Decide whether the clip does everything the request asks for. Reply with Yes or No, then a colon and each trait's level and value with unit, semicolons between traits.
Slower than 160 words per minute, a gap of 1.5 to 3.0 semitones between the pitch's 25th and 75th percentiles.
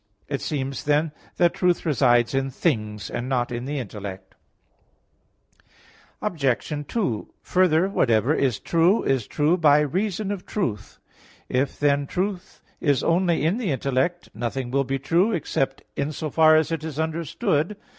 No: average, 150 wpm; average, 4.4 semitones